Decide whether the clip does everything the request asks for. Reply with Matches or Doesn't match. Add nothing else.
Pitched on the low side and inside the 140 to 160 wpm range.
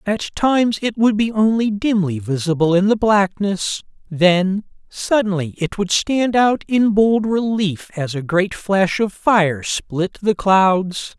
Doesn't match